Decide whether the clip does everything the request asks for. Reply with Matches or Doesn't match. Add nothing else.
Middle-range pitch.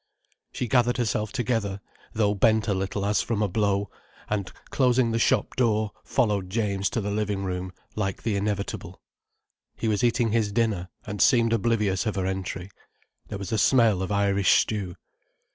Doesn't match